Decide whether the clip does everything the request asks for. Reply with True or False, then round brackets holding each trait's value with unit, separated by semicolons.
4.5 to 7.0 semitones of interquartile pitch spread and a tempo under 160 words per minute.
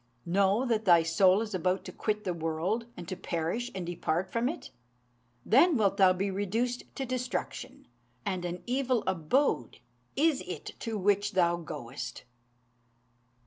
True (5.2 semitones; 150 wpm)